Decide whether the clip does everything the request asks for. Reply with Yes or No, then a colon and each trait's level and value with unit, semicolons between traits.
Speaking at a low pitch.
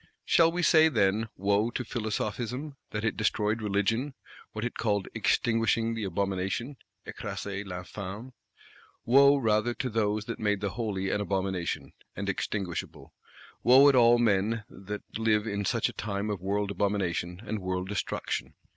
Yes: low, 105 Hz